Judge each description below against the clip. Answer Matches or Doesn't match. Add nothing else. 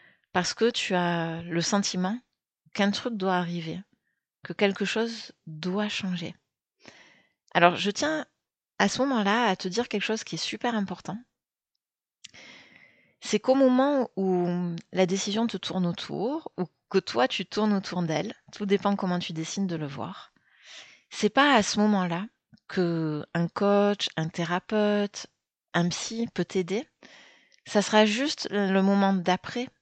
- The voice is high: Matches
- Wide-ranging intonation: Doesn't match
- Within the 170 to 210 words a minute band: Doesn't match